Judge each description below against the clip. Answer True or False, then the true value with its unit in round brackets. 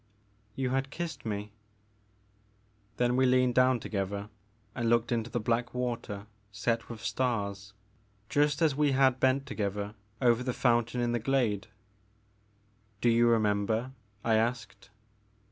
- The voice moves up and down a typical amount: True (3.5 semitones)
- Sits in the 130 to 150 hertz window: False (115 Hz)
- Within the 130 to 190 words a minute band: True (150 wpm)